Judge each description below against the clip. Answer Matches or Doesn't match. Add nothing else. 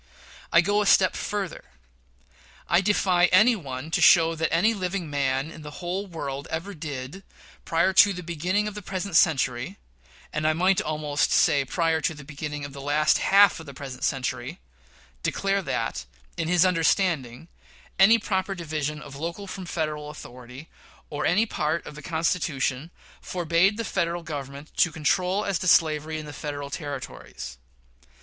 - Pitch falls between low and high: Matches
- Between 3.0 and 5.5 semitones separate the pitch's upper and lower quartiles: Matches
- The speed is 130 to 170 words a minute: Matches